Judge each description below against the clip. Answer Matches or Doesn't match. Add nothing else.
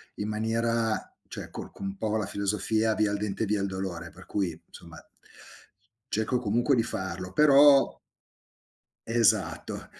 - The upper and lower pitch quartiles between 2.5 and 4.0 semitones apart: Matches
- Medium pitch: Doesn't match